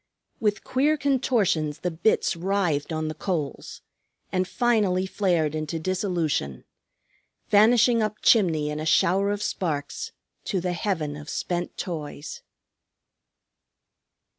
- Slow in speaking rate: Yes, slow, 115 wpm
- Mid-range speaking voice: Yes, medium, 180 Hz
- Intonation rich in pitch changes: No, average, 4.8 semitones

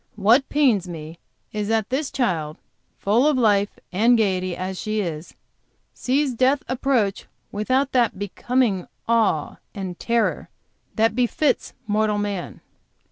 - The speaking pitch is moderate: No, high, 215 Hz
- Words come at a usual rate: No, slow, 130 wpm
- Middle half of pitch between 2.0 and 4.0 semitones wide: No, average, 4.7 semitones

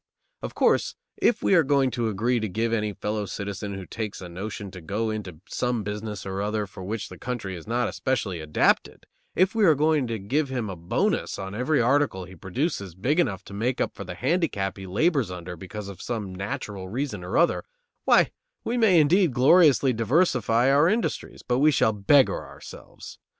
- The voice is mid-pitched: No, low, 110 Hz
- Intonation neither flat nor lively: No, wide, 6.0 semitones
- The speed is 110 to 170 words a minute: No, average, 195 wpm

